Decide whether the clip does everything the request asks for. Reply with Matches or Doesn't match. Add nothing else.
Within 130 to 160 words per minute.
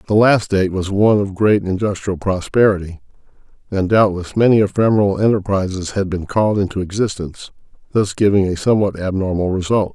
Matches